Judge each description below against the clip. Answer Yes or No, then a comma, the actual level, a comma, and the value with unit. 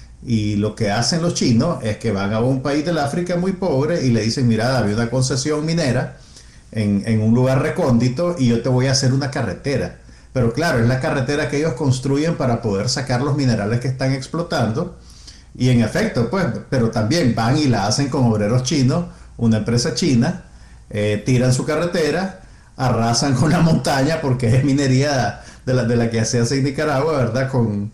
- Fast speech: Yes, fast, 195 wpm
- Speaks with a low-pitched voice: Yes, low, 130 Hz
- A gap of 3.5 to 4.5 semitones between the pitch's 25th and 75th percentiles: Yes, average, 3.9 semitones